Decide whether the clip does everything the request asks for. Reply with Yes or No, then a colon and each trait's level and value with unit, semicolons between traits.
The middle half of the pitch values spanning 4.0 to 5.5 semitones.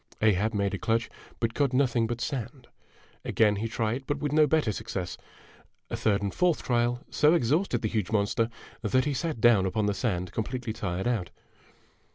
No: average, 3.6 semitones